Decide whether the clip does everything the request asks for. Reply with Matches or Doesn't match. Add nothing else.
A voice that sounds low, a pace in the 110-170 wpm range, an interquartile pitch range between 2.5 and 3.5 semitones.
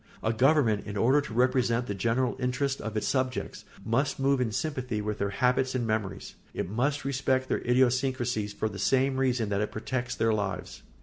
Doesn't match